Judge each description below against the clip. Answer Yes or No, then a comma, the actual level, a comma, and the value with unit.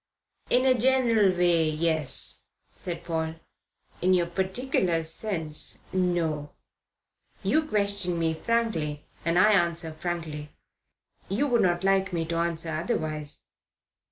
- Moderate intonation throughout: Yes, average, 3.8 semitones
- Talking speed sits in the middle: No, slow, 120 wpm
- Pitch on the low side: No, medium, 175 Hz